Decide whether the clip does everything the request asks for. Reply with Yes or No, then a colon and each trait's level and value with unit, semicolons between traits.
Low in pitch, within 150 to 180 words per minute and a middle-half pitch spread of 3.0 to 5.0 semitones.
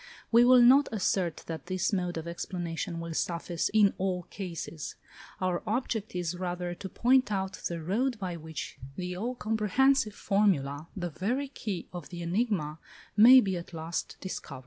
No: medium, 185 Hz; average, 165 wpm; average, 4.2 semitones